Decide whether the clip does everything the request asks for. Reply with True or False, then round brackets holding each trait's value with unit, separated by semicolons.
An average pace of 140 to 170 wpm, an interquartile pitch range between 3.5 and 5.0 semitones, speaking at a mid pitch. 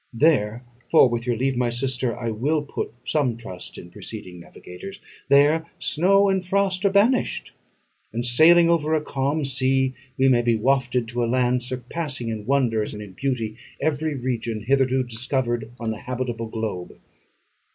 False (160 wpm; 4.0 semitones; 130 Hz)